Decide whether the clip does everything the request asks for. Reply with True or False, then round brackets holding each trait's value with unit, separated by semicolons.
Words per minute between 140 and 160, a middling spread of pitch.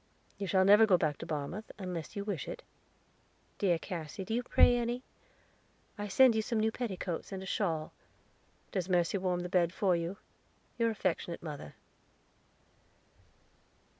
True (155 wpm; 3.8 semitones)